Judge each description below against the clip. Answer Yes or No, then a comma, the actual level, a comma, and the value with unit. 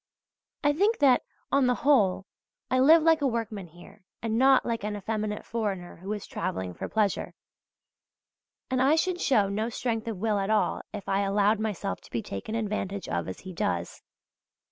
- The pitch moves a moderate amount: Yes, average, 4.6 semitones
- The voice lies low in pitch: No, high, 215 Hz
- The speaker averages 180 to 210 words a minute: Yes, average, 185 wpm